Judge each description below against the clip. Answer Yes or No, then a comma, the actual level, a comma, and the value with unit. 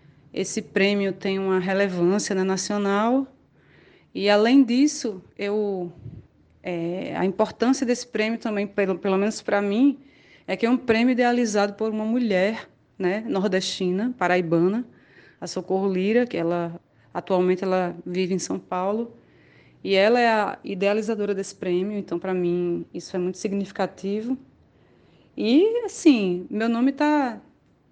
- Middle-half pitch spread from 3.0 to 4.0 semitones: Yes, average, 3.7 semitones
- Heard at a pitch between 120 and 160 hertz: No, high, 200 Hz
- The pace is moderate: Yes, average, 140 wpm